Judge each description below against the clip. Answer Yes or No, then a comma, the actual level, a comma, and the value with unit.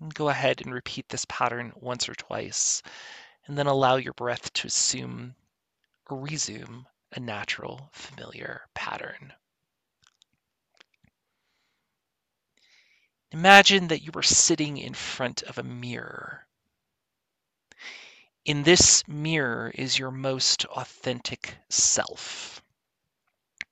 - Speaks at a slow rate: Yes, slow, 100 wpm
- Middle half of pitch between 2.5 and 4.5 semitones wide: Yes, average, 3.8 semitones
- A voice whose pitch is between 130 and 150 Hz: Yes, low, 135 Hz